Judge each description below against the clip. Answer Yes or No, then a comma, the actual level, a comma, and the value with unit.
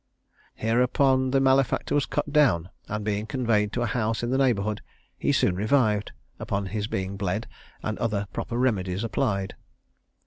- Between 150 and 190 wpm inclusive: Yes, average, 160 wpm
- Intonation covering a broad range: No, average, 4.1 semitones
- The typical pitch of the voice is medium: No, low, 110 Hz